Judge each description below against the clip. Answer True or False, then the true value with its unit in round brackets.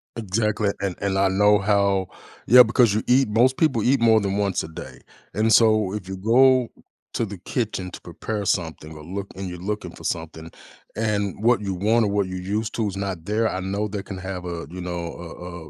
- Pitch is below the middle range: True (100 Hz)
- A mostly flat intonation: False (3.0 semitones)